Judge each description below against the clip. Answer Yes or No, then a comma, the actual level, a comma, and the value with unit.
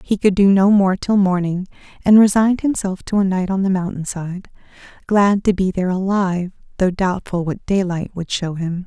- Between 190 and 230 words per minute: Yes, average, 195 wpm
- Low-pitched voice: No, high, 190 Hz